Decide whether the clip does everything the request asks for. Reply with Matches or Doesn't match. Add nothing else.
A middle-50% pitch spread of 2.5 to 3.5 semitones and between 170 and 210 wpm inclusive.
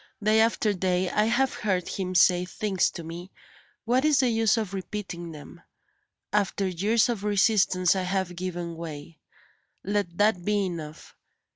Doesn't match